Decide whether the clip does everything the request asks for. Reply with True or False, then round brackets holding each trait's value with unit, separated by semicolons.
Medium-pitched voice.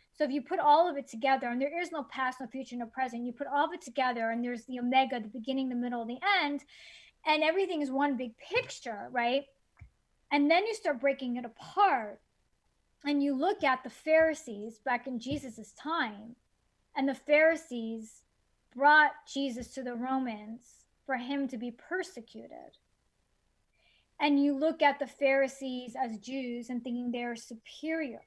False (265 Hz)